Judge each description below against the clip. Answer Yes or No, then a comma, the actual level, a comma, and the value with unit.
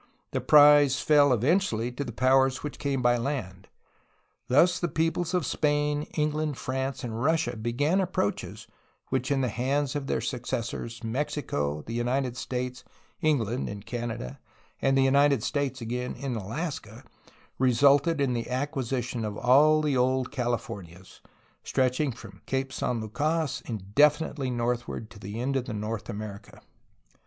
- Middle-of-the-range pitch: No, low, 130 Hz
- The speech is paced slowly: No, average, 150 wpm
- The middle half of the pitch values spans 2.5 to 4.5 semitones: Yes, average, 3.7 semitones